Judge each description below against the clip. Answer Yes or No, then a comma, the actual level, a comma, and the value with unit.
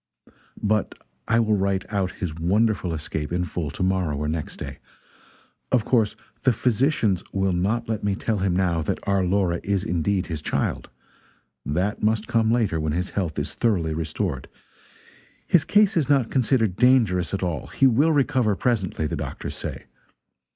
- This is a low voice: Yes, low, 100 Hz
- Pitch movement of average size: Yes, average, 4.6 semitones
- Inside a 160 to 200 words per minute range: Yes, average, 170 wpm